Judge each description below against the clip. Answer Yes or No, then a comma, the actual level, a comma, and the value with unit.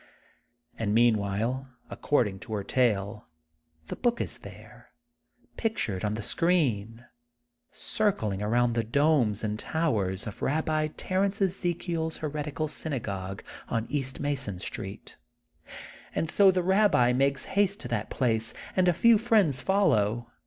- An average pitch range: No, wide, 7.5 semitones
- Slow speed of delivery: Yes, slow, 130 wpm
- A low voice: Yes, low, 130 Hz